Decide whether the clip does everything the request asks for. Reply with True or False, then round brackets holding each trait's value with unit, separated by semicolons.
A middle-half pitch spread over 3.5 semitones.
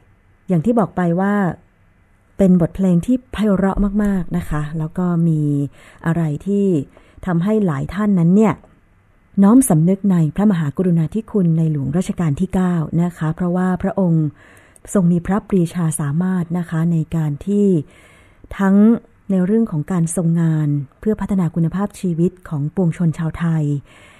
True (4.2 semitones)